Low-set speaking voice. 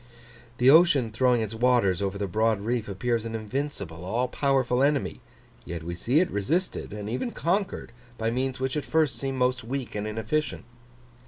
Yes: low, 120 Hz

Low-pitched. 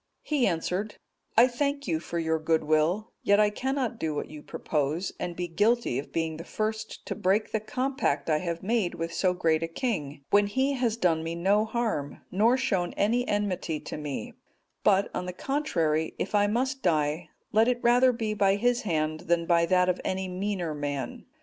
No: high, 190 Hz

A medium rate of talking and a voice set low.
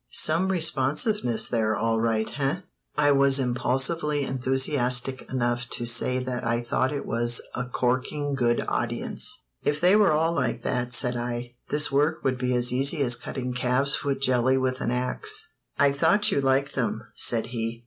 Yes: average, 170 wpm; low, 130 Hz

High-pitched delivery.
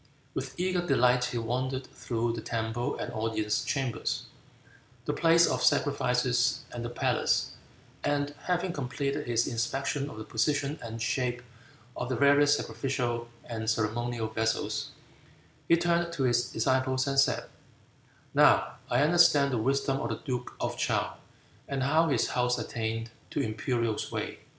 No: low, 125 Hz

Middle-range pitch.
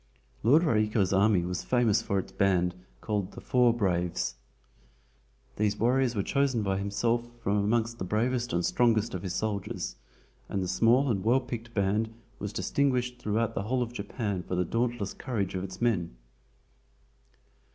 No: low, 110 Hz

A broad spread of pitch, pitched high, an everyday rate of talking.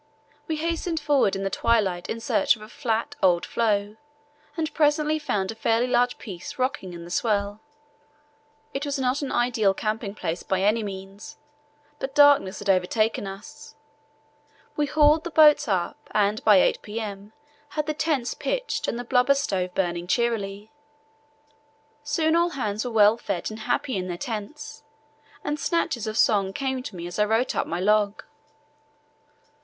Yes: wide, 6.1 semitones; high, 225 Hz; average, 165 wpm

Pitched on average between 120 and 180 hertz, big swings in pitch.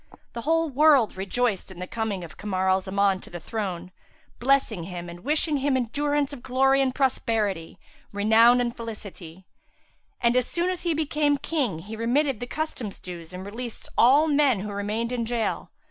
No: high, 235 Hz; wide, 6.0 semitones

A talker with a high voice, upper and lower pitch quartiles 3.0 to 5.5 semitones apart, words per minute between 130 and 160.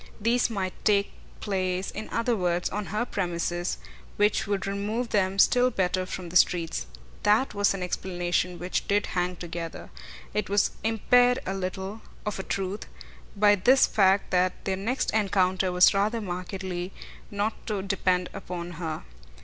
No: high, 195 Hz; narrow, 2.4 semitones; average, 155 wpm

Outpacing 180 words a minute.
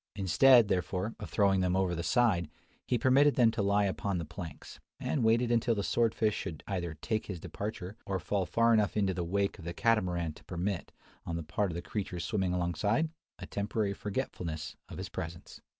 Yes: average, 200 wpm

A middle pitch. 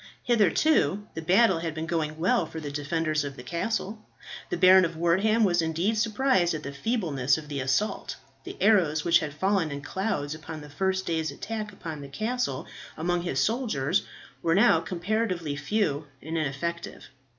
Yes: medium, 170 Hz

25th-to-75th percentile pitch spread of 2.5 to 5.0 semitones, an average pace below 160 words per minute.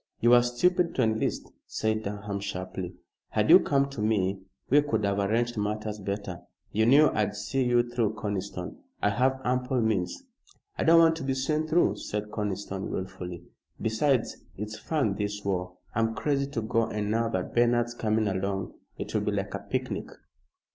No: average, 3.7 semitones; average, 175 wpm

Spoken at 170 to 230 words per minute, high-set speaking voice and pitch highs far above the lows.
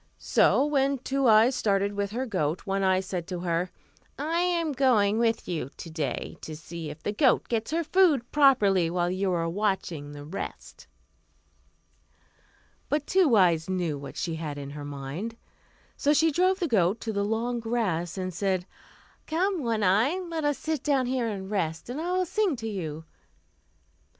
Yes: average, 180 wpm; high, 210 Hz; wide, 7.9 semitones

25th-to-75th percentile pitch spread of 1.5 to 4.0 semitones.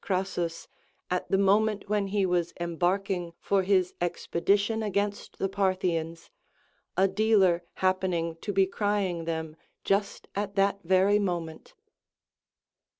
Yes: narrow, 2.5 semitones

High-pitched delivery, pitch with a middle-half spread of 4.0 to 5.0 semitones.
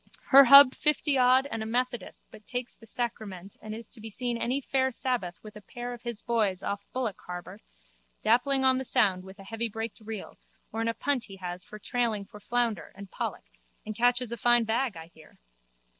No: high, 230 Hz; average, 3.4 semitones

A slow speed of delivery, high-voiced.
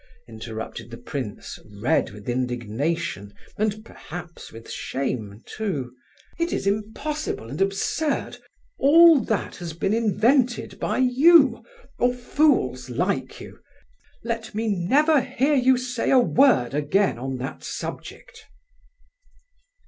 Yes: slow, 120 wpm; high, 200 Hz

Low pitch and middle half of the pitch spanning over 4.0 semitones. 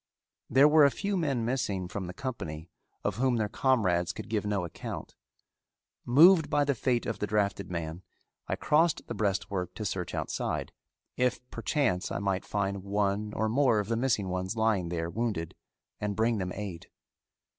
Yes: low, 105 Hz; average, 5.0 semitones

